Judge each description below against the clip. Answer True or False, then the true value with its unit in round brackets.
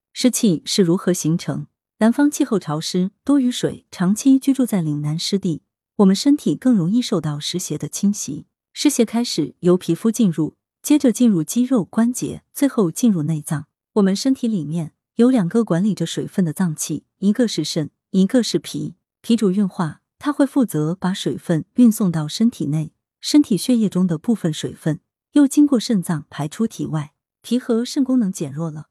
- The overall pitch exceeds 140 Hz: True (190 Hz)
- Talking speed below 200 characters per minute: False (270 characters per minute)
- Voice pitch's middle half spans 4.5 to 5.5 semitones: False (6.8 semitones)